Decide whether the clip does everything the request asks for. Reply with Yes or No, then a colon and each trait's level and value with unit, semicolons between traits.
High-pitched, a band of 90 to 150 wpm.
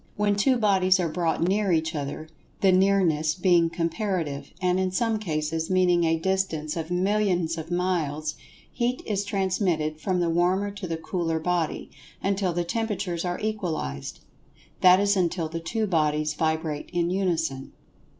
No: medium, 175 Hz; average, 145 wpm